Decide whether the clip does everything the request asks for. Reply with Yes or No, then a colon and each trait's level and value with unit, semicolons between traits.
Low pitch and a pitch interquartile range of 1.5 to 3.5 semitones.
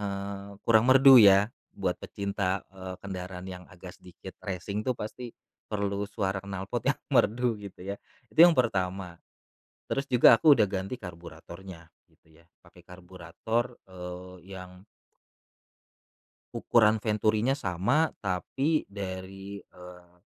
Yes: low, 100 Hz; average, 2.9 semitones